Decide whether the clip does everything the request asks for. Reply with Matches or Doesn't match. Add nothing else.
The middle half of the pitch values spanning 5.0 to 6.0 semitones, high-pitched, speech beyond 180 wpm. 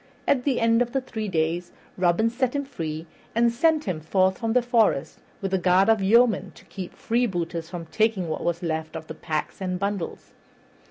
Matches